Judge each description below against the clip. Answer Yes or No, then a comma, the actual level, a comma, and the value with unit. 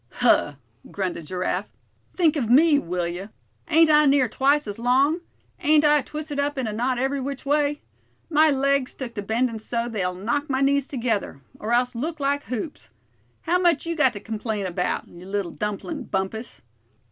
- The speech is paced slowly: No, average, 180 wpm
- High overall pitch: Yes, very high, 255 Hz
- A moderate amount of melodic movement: No, wide, 5.7 semitones